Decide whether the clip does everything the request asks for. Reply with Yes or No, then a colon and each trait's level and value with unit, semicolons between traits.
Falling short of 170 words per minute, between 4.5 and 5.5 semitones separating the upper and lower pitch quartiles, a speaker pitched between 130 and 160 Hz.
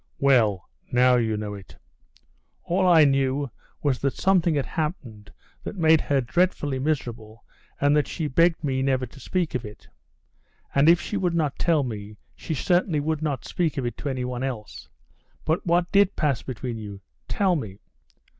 No: average, 175 wpm; average, 5.2 semitones; medium, 140 Hz